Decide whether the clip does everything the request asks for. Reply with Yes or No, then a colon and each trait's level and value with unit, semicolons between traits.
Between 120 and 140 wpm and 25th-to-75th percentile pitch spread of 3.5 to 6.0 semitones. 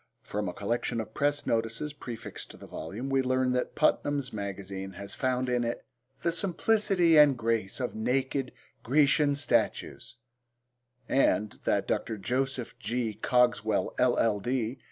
Yes: slow, 135 wpm; average, 3.8 semitones